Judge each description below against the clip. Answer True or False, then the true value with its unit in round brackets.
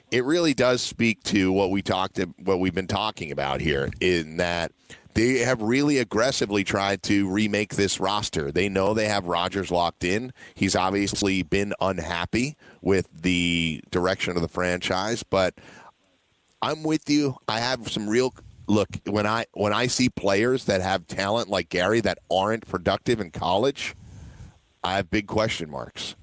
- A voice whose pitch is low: True (100 Hz)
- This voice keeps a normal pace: True (165 wpm)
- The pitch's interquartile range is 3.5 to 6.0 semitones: False (3.1 semitones)